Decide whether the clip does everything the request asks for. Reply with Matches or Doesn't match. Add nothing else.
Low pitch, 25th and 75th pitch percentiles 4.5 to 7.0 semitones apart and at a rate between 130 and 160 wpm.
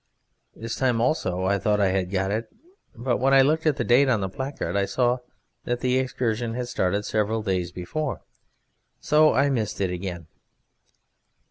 Doesn't match